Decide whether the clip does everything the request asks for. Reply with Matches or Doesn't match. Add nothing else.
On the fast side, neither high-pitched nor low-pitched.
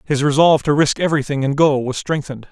Matches